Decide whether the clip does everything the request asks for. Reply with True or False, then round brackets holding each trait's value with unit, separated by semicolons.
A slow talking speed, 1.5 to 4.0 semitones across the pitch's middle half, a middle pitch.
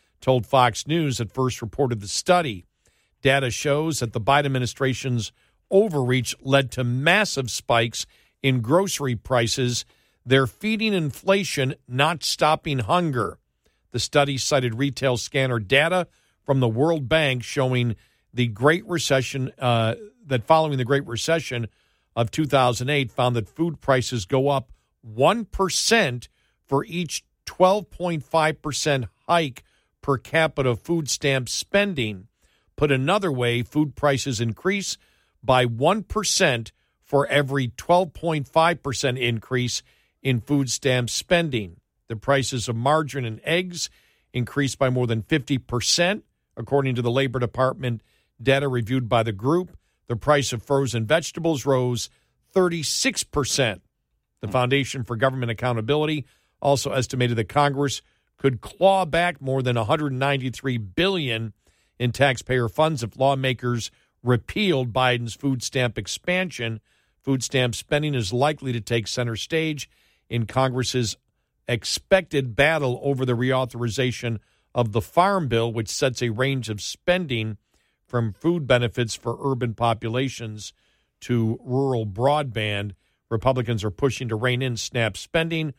False (125 wpm; 3.7 semitones; 130 Hz)